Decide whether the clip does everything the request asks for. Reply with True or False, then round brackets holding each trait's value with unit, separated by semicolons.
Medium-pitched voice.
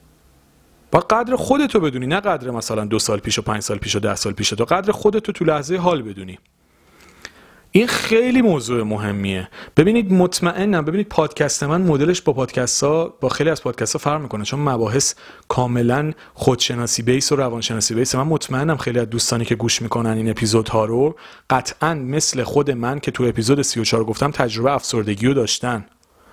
False (130 Hz)